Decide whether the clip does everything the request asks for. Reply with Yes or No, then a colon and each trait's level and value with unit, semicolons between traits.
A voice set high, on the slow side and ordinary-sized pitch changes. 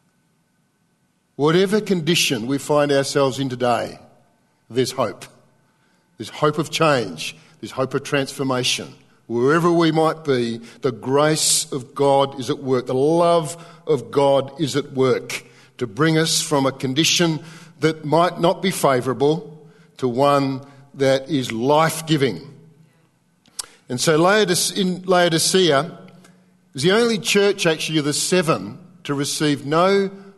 No: medium, 150 Hz; slow, 130 wpm; average, 3.6 semitones